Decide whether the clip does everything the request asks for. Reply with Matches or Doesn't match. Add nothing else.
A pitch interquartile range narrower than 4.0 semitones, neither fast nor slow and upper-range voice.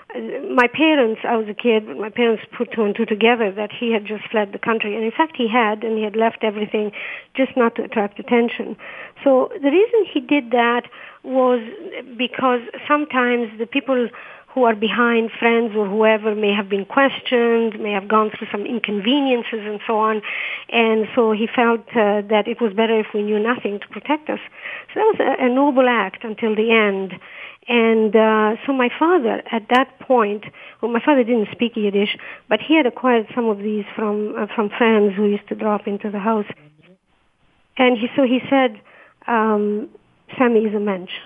Matches